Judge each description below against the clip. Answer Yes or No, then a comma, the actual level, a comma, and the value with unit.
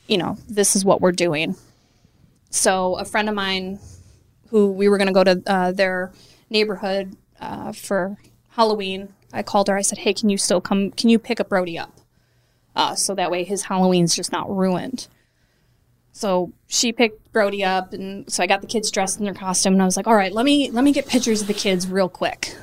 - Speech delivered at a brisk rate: Yes, fast, 215 wpm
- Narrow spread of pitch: Yes, narrow, 1.9 semitones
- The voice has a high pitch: Yes, high, 195 Hz